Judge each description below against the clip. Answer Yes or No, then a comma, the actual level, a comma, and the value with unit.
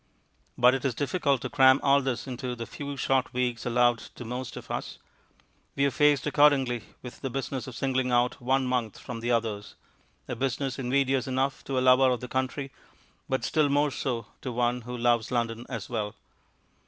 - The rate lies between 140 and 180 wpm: No, average, 190 wpm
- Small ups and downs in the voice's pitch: Yes, narrow, 2.0 semitones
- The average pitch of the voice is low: Yes, low, 130 Hz